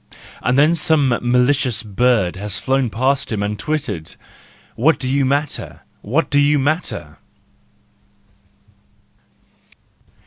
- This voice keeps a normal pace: No, slow, 115 wpm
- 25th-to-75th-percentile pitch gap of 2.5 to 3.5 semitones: No, average, 4.6 semitones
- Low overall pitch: Yes, low, 130 Hz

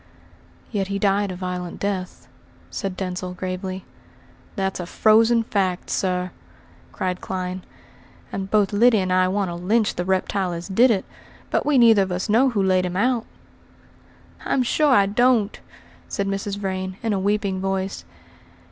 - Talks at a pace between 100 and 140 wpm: No, average, 160 wpm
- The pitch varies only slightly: Yes, narrow, 2.3 semitones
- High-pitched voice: Yes, high, 195 Hz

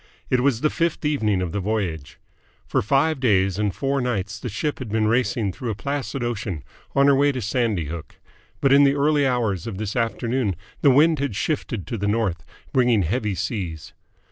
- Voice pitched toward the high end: No, low, 115 Hz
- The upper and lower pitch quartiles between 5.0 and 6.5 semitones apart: Yes, wide, 5.4 semitones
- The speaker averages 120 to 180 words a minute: No, average, 195 wpm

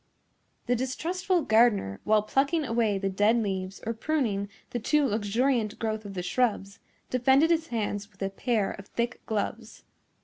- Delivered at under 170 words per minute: Yes, average, 160 wpm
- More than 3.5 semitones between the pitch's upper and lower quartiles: Yes, average, 3.9 semitones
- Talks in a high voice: Yes, high, 225 Hz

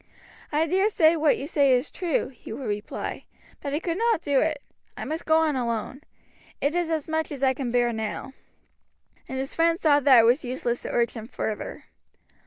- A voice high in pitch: Yes, very high, 285 Hz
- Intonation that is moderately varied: Yes, average, 4.4 semitones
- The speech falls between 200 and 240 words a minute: Yes, fast, 205 wpm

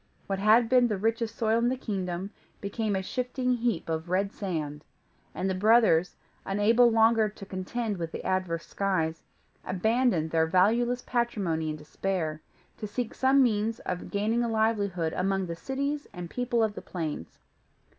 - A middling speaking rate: Yes, average, 165 wpm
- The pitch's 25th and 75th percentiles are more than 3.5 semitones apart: Yes, average, 4.5 semitones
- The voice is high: Yes, high, 205 Hz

